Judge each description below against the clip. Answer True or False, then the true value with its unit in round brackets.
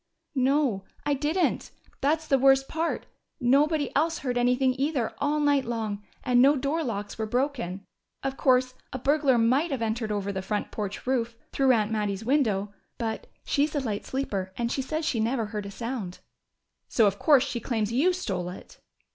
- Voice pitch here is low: False (250 Hz)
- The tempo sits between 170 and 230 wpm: True (180 wpm)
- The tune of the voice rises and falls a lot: False (4.6 semitones)